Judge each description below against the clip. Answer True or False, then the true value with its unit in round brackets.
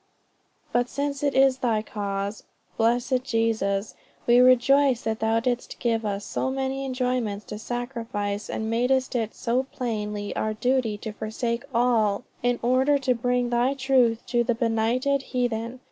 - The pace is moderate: True (155 wpm)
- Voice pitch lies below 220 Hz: False (240 Hz)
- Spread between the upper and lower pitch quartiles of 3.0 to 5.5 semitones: False (2.6 semitones)